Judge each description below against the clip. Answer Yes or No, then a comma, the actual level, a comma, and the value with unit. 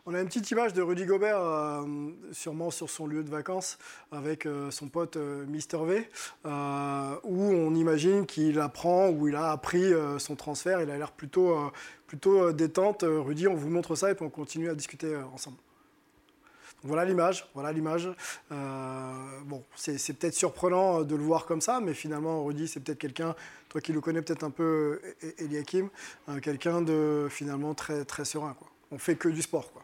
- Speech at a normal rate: Yes, average, 180 wpm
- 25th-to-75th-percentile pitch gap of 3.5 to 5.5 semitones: No, narrow, 2.6 semitones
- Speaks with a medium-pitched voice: Yes, medium, 155 Hz